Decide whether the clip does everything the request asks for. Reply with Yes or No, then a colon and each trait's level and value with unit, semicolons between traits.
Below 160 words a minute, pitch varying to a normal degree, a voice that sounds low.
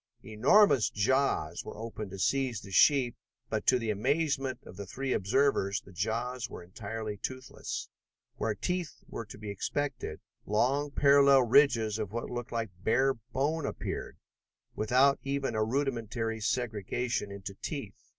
Yes: average, 145 wpm; average, 4.4 semitones; low, 120 Hz